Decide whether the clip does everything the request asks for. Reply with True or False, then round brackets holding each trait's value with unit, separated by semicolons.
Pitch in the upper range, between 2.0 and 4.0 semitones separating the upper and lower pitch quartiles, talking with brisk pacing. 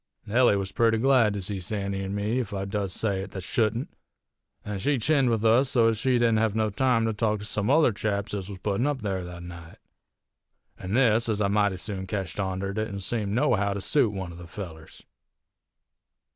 False (105 Hz; 2.8 semitones; 215 wpm)